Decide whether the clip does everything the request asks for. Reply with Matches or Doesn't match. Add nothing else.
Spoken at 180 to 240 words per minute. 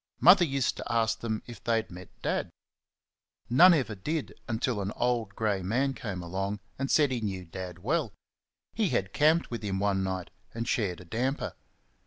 Matches